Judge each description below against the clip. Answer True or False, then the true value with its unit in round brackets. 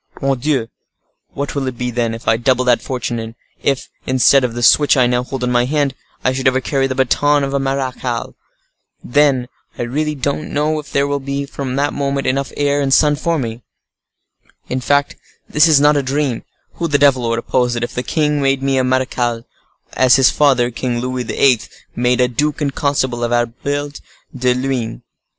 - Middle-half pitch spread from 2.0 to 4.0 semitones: True (2.4 semitones)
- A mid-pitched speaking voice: False (130 Hz)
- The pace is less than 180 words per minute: False (205 wpm)